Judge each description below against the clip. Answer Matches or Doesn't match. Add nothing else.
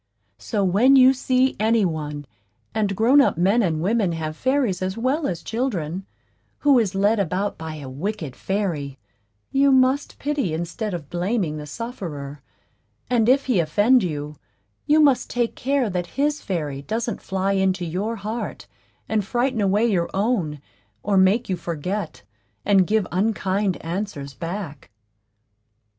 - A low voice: Doesn't match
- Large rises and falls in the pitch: Matches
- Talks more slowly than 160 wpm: Matches